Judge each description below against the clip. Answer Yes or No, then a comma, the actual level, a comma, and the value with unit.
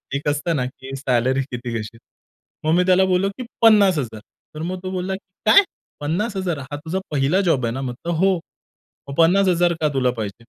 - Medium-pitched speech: Yes, medium, 155 Hz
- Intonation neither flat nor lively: No, wide, 6.1 semitones